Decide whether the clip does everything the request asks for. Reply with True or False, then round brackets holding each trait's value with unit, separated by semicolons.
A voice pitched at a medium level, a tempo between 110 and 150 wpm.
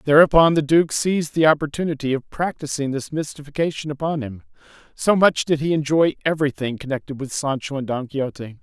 False (145 Hz; 165 wpm)